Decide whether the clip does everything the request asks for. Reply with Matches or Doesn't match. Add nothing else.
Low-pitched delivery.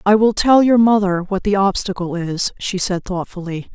Doesn't match